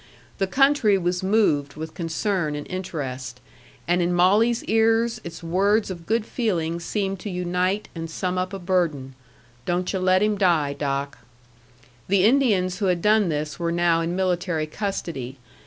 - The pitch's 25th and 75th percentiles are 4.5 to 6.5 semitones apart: No, average, 3.4 semitones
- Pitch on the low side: No, medium, 180 Hz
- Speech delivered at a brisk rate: No, average, 160 wpm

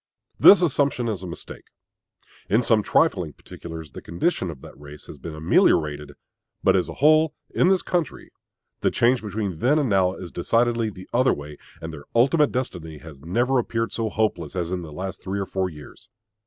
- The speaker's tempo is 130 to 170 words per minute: No, average, 190 wpm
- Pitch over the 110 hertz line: No, very low, 95 Hz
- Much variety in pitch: Yes, wide, 7.0 semitones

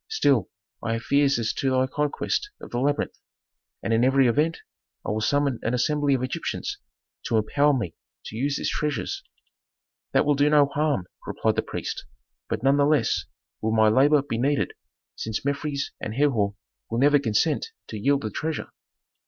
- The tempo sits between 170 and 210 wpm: Yes, average, 175 wpm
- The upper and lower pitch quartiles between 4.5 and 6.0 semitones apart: No, average, 4.1 semitones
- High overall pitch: No, medium, 140 Hz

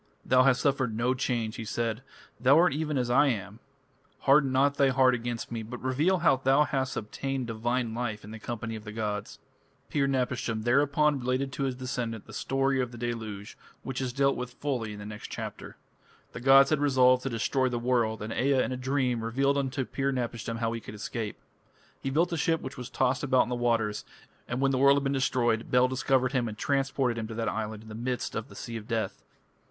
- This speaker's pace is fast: Yes, fast, 220 wpm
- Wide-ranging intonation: No, average, 2.9 semitones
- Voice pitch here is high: No, low, 125 Hz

